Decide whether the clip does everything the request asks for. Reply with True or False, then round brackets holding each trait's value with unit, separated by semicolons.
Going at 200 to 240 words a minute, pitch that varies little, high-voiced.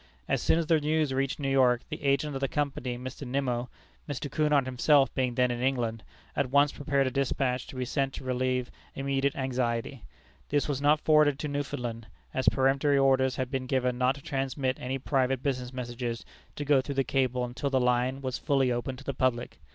False (205 wpm; 1.7 semitones; 130 Hz)